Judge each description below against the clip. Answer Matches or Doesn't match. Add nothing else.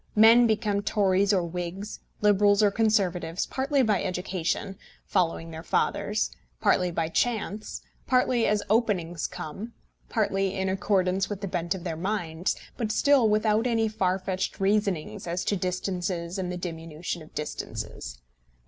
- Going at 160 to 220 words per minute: Doesn't match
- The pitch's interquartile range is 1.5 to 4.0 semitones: Matches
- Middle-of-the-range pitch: Doesn't match